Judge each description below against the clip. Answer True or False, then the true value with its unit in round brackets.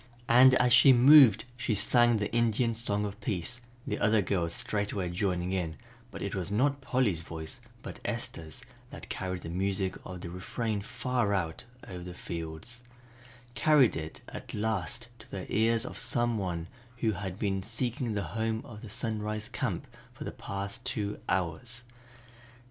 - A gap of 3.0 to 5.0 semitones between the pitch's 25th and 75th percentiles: True (4.4 semitones)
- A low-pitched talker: True (105 Hz)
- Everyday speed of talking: True (165 wpm)